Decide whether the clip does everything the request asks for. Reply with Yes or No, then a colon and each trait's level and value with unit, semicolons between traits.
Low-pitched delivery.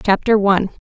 No: high, 200 Hz